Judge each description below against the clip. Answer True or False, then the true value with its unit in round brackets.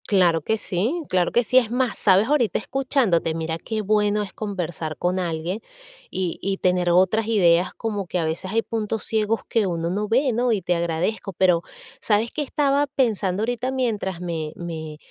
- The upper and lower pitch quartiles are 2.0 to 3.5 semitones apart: False (4.6 semitones)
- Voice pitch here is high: True (200 Hz)